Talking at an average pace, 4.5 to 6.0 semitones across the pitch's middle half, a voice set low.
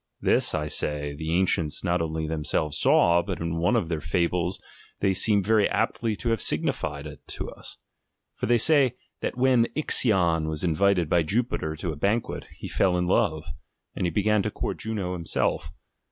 Yes: average, 180 wpm; average, 5.1 semitones; very low, 90 Hz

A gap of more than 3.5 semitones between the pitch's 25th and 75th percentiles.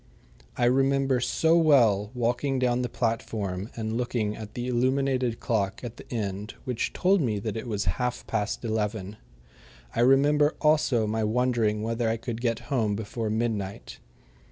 No: average, 2.9 semitones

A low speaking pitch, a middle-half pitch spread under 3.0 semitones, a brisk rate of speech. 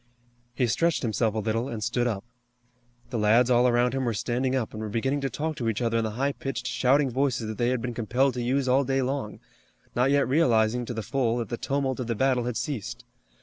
Yes: low, 125 Hz; narrow, 2.6 semitones; fast, 240 wpm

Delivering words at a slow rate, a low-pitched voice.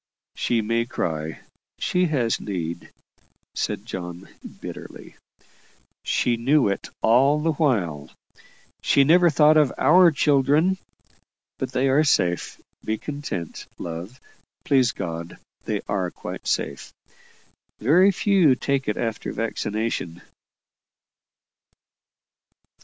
Yes: slow, 105 wpm; low, 125 Hz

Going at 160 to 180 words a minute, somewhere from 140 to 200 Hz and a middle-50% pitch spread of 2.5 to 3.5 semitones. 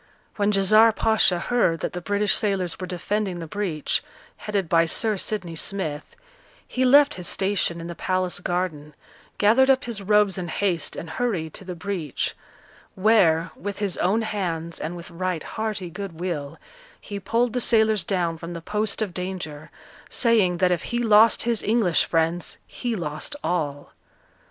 No: average, 165 wpm; medium, 185 Hz; average, 4.0 semitones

